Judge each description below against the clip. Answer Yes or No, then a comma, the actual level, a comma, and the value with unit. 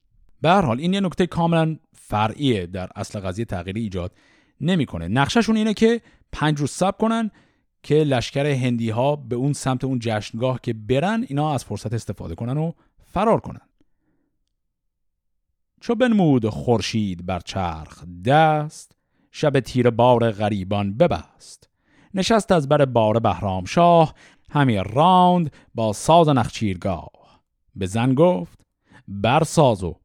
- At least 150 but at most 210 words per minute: No, average, 135 wpm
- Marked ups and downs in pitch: Yes, wide, 7.4 semitones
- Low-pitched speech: Yes, low, 120 Hz